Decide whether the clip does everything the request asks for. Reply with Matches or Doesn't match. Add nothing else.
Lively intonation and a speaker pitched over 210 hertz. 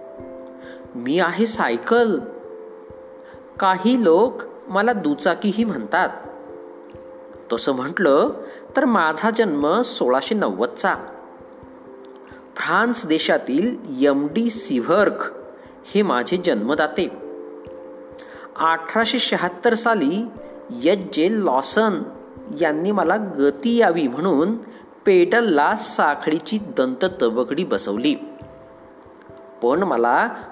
Matches